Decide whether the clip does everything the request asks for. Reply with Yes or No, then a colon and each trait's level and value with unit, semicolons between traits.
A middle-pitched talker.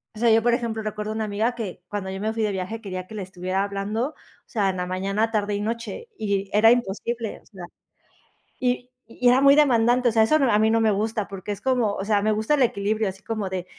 No: high, 215 Hz